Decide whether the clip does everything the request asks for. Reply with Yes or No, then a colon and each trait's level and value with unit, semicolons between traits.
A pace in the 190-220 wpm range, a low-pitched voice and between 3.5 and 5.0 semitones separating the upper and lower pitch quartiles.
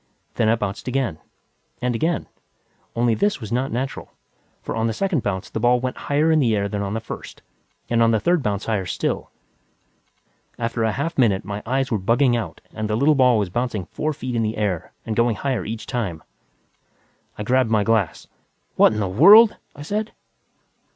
Yes: average, 195 wpm; low, 115 Hz; average, 3.9 semitones